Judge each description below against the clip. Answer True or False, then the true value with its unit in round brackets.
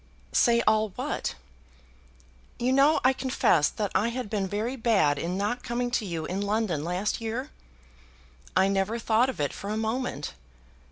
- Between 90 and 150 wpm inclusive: False (165 wpm)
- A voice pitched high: True (220 Hz)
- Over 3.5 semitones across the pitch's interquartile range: True (4.0 semitones)